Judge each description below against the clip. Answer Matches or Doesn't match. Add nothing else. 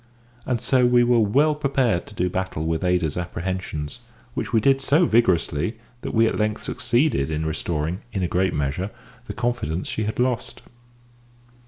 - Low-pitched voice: Matches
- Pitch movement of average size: Doesn't match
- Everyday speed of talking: Matches